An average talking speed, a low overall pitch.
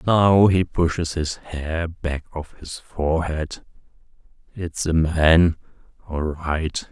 No: slow, 115 wpm; very low, 80 Hz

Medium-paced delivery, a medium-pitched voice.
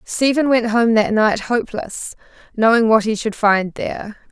No: average, 165 wpm; high, 225 Hz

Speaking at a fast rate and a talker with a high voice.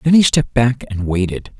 No: fast, 225 wpm; low, 120 Hz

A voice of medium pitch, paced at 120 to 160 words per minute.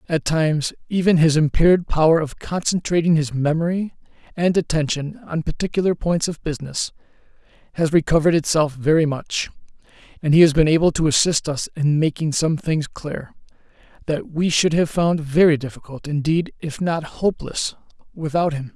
Yes: medium, 160 Hz; average, 155 wpm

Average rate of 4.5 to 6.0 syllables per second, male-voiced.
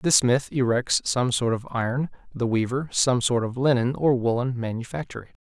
Yes: 5.0 syllables/s; male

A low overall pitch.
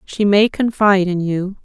No: high, 195 Hz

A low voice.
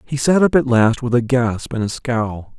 Yes: low, 125 Hz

